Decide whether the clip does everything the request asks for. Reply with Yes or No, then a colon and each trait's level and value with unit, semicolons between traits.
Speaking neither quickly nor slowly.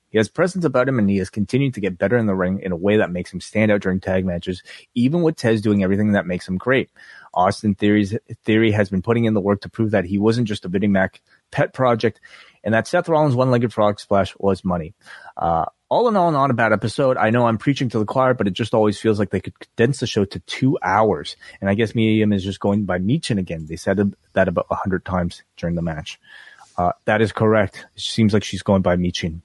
No: fast, 255 wpm